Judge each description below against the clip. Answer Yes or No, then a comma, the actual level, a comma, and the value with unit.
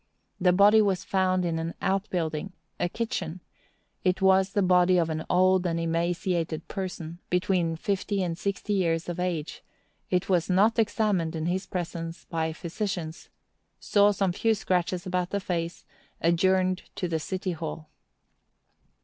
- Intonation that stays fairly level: Yes, narrow, 2.3 semitones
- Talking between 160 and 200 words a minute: No, average, 145 wpm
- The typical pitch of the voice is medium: Yes, medium, 180 Hz